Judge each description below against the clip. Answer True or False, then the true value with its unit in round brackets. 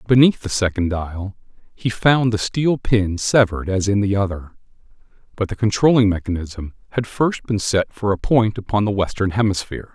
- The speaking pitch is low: True (105 Hz)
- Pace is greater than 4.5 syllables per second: True (5.1 syllables/s)